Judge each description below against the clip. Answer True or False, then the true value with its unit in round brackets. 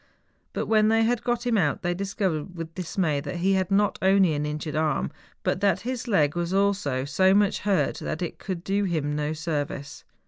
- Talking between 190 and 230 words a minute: True (205 wpm)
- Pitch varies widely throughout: False (4.6 semitones)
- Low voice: False (185 Hz)